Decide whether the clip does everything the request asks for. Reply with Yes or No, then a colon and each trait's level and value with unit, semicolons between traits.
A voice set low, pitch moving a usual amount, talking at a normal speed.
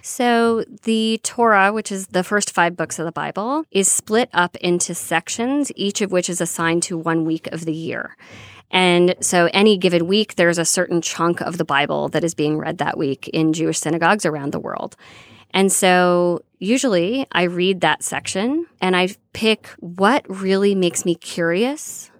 No: medium, 180 Hz; average, 3.5 semitones; average, 180 wpm